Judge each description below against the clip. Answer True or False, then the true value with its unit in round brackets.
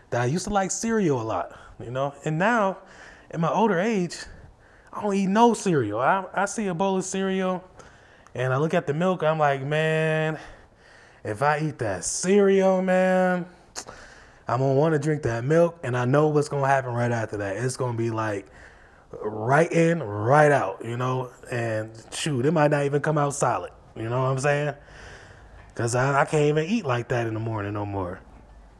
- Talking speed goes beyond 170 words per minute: True (200 wpm)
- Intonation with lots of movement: True (6.8 semitones)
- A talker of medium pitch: True (145 Hz)